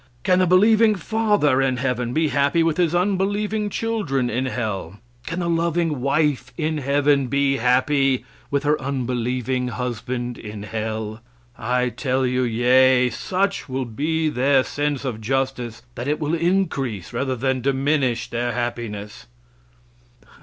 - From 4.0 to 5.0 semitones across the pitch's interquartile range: Yes, average, 4.3 semitones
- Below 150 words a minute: Yes, average, 140 wpm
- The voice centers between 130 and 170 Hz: Yes, low, 135 Hz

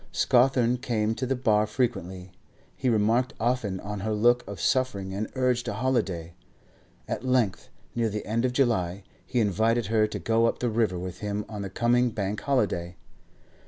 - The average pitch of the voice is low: Yes, low, 110 Hz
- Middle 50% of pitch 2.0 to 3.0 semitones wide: No, average, 3.4 semitones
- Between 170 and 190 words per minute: Yes, average, 175 wpm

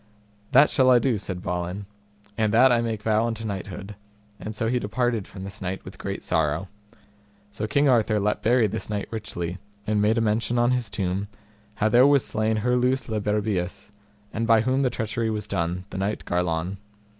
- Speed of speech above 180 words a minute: Yes, average, 190 wpm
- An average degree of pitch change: Yes, average, 3.2 semitones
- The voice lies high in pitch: No, low, 110 Hz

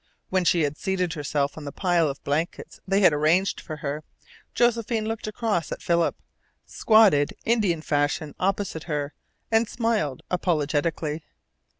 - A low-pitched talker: No, medium, 170 Hz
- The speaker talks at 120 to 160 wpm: Yes, average, 140 wpm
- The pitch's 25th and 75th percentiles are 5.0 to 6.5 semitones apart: Yes, wide, 5.4 semitones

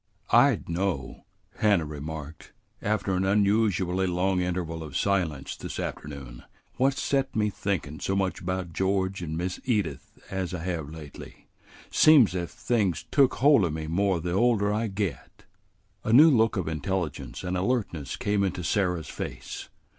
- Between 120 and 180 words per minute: Yes, average, 155 wpm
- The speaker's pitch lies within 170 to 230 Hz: No, very low, 95 Hz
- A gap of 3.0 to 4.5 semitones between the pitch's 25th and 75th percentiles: Yes, average, 4.1 semitones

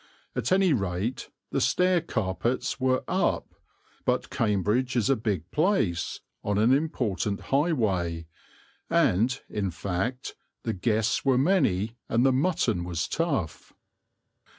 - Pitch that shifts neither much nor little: No, wide, 5.9 semitones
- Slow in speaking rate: Yes, slow, 125 wpm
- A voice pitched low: Yes, low, 115 Hz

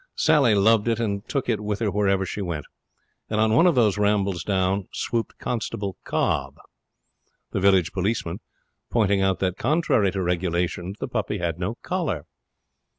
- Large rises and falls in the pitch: No, average, 3.2 semitones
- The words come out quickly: No, average, 160 wpm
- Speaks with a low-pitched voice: Yes, low, 100 Hz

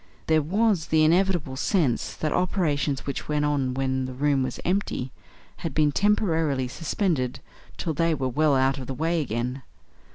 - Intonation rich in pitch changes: No, average, 4.1 semitones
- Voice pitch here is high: No, medium, 150 Hz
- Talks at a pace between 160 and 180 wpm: Yes, average, 165 wpm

